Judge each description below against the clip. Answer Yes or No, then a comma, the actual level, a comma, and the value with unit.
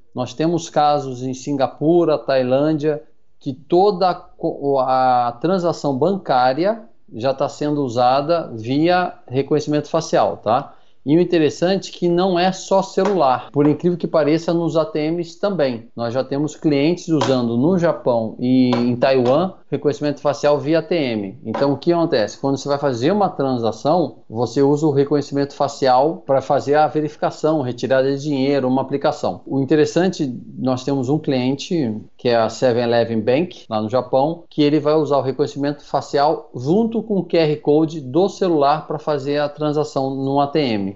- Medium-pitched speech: Yes, medium, 145 Hz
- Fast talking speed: No, average, 155 wpm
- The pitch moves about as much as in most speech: Yes, average, 3.7 semitones